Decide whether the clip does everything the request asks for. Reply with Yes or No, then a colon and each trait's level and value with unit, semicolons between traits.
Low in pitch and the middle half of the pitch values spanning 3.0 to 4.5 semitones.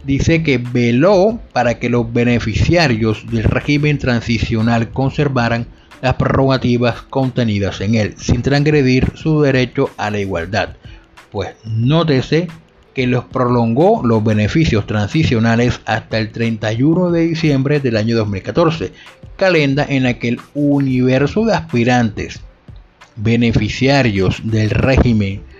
Yes: low, 120 Hz; average, 3.7 semitones